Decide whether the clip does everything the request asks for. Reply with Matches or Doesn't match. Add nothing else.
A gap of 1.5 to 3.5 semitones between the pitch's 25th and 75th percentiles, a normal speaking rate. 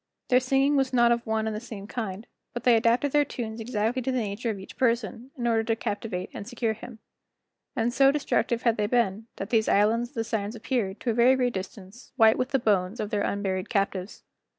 Doesn't match